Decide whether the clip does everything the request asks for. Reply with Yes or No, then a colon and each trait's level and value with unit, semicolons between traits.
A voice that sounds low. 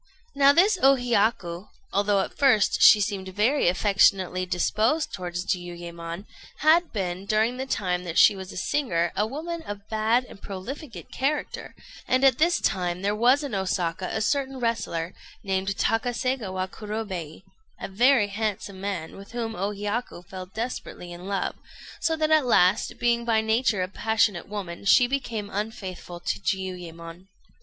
No: high, 205 Hz